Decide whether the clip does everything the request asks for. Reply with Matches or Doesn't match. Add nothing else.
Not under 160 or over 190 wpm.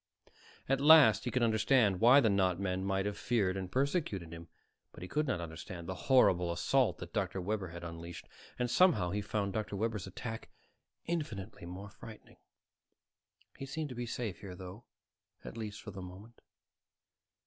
Matches